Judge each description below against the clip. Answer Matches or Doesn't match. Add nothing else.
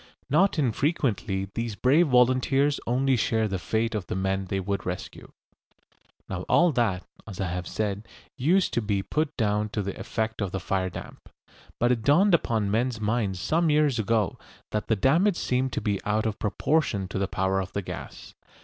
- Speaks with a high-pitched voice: Doesn't match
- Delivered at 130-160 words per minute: Doesn't match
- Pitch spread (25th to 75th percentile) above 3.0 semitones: Matches